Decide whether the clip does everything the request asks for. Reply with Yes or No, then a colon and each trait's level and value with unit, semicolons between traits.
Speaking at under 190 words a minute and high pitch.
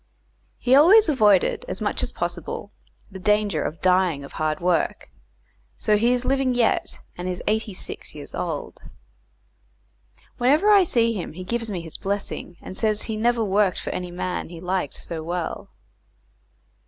Yes: average, 165 wpm; high, 205 Hz